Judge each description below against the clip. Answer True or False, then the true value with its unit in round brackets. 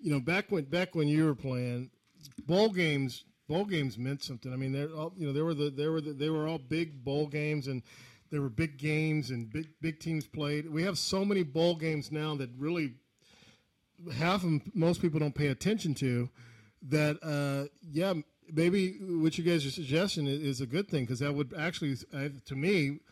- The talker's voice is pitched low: False (150 Hz)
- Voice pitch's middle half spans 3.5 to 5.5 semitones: False (3.0 semitones)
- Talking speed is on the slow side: False (205 wpm)